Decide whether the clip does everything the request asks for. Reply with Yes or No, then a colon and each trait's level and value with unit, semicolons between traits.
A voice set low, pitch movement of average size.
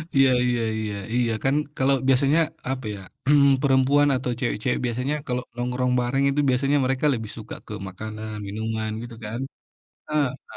Yes: low, 125 Hz; average, 3.2 semitones